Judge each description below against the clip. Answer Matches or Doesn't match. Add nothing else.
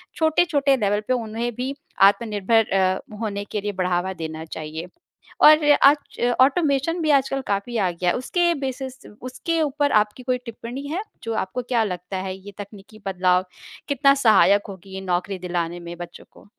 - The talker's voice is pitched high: Matches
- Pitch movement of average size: Doesn't match